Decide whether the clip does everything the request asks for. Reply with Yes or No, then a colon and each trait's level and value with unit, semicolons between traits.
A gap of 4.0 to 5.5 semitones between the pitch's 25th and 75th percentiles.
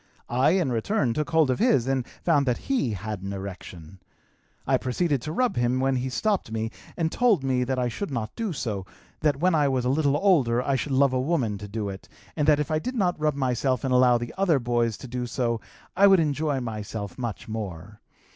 Yes: average, 4.8 semitones